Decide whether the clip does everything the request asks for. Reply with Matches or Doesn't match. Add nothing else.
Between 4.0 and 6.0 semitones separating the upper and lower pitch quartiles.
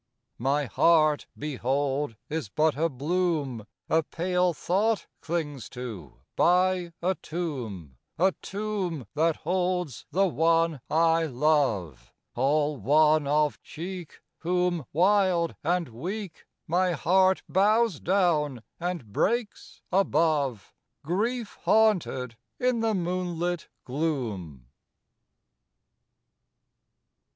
Matches